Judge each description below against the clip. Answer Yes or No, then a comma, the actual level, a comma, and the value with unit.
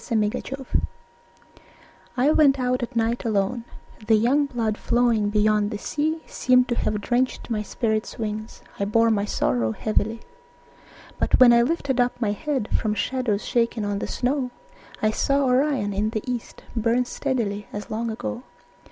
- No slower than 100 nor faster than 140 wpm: No, average, 160 wpm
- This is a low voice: No, high, 230 Hz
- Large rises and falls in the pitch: No, average, 3.1 semitones